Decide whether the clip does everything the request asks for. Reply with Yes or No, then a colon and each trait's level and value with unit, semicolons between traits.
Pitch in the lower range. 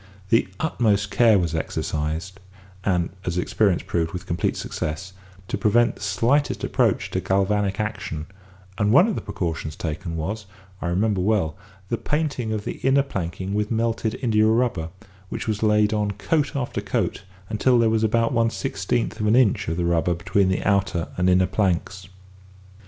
Yes: low, 105 Hz